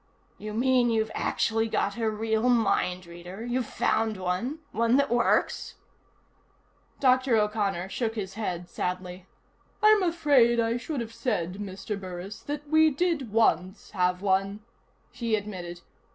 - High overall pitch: Yes, high, 220 Hz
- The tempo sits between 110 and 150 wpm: Yes, average, 140 wpm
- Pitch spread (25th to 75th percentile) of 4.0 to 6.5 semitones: Yes, average, 4.3 semitones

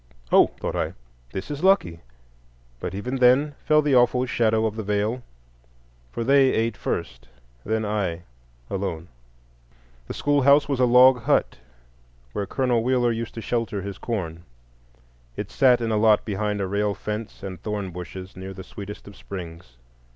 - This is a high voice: No, low, 105 Hz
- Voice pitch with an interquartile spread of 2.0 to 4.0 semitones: No, average, 4.6 semitones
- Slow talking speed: No, average, 160 wpm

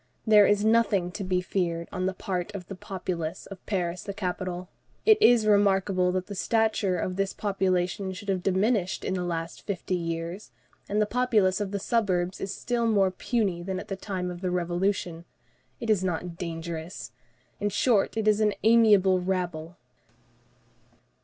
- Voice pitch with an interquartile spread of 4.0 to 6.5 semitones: No, narrow, 2.5 semitones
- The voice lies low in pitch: No, high, 190 Hz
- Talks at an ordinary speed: Yes, average, 170 wpm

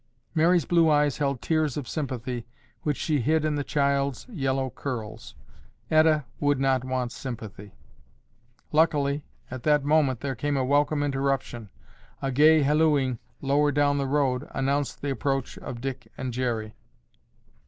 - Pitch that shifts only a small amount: Yes, narrow, 2.3 semitones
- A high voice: No, medium, 140 Hz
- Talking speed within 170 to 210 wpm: No, average, 145 wpm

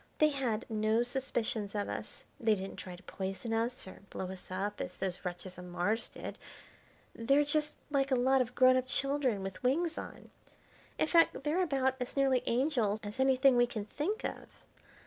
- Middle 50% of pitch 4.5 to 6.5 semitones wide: Yes, average, 4.9 semitones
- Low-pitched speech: No, high, 245 Hz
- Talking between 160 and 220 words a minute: Yes, average, 185 wpm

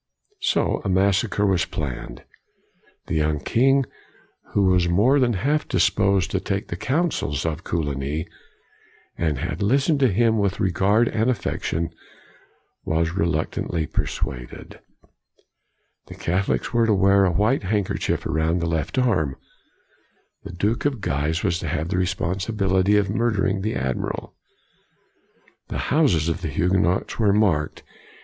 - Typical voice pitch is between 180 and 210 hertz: No, very low, 95 Hz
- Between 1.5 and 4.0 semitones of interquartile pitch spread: No, average, 4.7 semitones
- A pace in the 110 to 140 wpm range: Yes, slow, 135 wpm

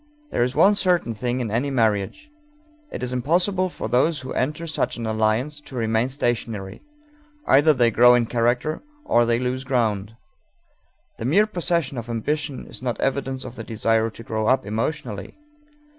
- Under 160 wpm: No, average, 170 wpm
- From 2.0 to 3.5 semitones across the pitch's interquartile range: No, average, 4.3 semitones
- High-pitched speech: No, low, 125 Hz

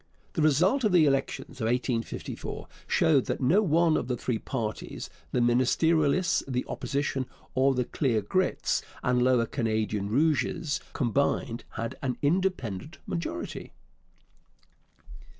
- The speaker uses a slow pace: Yes, slow, 125 wpm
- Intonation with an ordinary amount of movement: Yes, average, 4.9 semitones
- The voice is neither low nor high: No, low, 130 Hz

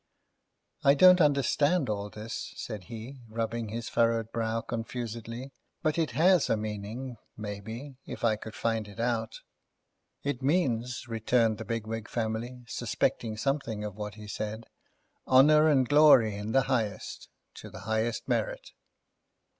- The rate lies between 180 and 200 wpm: No, average, 140 wpm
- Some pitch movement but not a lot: Yes, average, 3.4 semitones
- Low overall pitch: Yes, low, 115 Hz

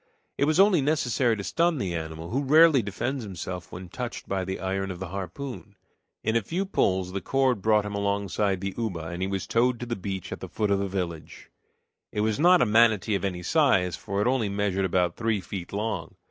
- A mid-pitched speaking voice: No, low, 100 Hz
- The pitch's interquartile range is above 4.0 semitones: Yes, average, 4.5 semitones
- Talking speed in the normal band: No, fast, 220 wpm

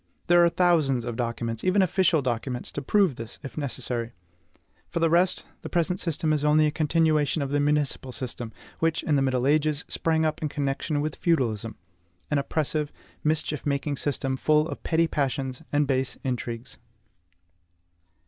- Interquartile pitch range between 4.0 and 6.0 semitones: No, average, 3.4 semitones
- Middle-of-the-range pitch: Yes, medium, 145 Hz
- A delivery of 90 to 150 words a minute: No, average, 165 wpm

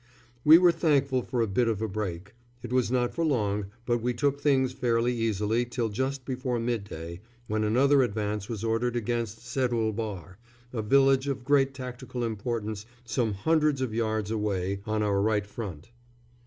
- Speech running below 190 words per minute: Yes, average, 170 wpm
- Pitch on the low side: Yes, low, 115 Hz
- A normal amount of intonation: Yes, average, 3.5 semitones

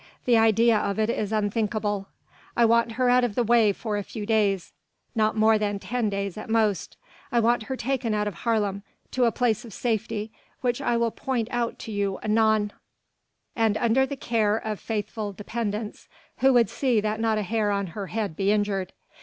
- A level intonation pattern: Yes, narrow, 2.1 semitones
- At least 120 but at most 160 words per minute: No, average, 195 wpm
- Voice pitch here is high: Yes, high, 220 Hz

